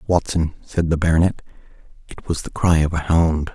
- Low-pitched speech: Yes, very low, 80 Hz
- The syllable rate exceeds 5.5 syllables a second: No, 5.3 syllables/s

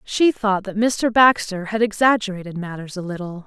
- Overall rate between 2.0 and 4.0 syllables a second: No, 5.0 syllables/s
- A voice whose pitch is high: Yes, high, 205 Hz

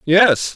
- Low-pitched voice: No, medium, 175 Hz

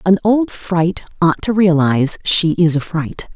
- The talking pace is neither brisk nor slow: Yes, average, 180 wpm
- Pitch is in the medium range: Yes, medium, 175 Hz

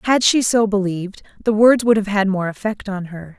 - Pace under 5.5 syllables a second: Yes, 5.3 syllables/s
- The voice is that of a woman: Yes, female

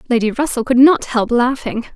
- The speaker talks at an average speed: Yes, average, 185 wpm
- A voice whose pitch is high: Yes, high, 245 Hz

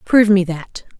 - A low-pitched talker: No, high, 195 Hz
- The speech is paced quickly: No, average, 180 wpm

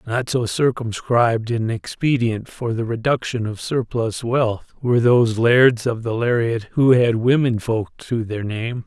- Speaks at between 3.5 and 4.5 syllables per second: Yes, 4.2 syllables/s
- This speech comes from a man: Yes, male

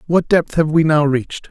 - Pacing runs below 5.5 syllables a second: Yes, 5.2 syllables/s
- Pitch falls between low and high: Yes, medium, 155 Hz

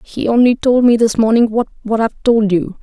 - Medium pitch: No, high, 225 Hz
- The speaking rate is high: Yes, fast, 210 wpm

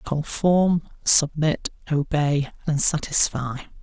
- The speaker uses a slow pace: Yes, slow, 80 wpm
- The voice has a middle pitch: Yes, medium, 150 Hz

